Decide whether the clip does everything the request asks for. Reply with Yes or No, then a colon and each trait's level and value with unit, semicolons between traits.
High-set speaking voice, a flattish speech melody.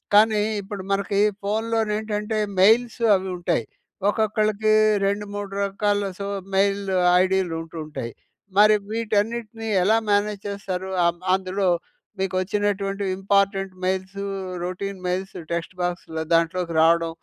Yes: high, 200 Hz; narrow, 2.0 semitones